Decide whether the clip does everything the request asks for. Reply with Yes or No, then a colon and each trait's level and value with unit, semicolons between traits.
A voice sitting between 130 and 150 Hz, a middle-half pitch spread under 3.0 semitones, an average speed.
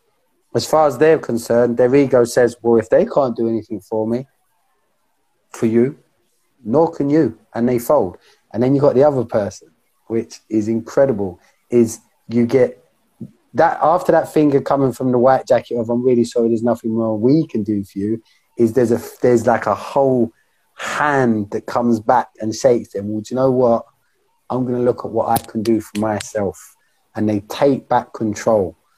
No: low, 120 Hz; narrow, 2.5 semitones; average, 195 wpm